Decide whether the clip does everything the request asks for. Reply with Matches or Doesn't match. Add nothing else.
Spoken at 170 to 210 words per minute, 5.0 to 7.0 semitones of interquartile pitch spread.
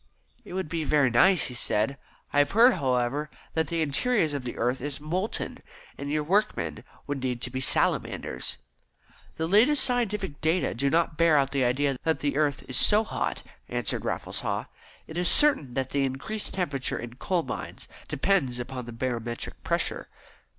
Matches